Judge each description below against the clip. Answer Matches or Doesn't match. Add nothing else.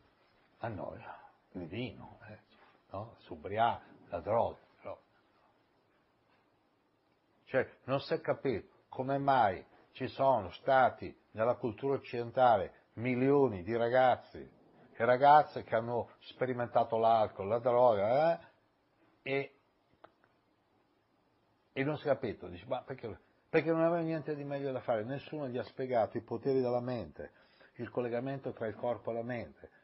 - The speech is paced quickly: Doesn't match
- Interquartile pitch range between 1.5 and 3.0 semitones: Matches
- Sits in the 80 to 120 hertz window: Doesn't match